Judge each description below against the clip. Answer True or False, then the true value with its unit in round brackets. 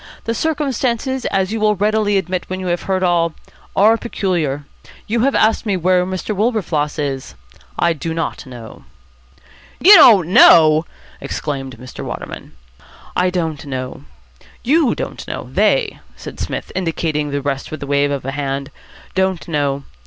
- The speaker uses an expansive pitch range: True (6.6 semitones)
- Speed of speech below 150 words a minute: False (155 wpm)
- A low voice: False (175 Hz)